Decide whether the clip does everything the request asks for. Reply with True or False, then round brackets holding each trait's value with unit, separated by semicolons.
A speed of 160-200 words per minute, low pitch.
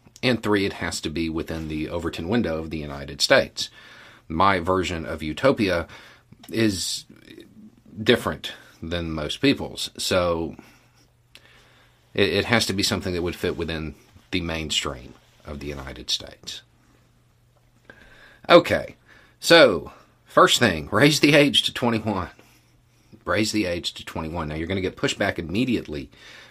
False (140 wpm; 85 Hz)